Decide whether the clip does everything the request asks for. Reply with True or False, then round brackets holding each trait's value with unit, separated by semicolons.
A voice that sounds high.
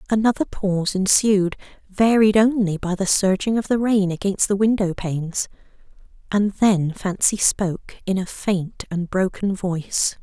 True (195 Hz)